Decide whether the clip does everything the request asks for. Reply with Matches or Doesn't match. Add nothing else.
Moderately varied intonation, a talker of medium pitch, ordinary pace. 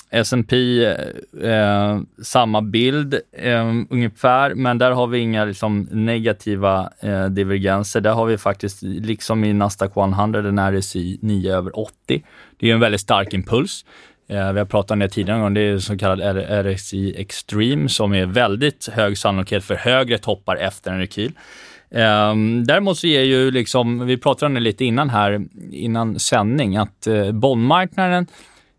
Doesn't match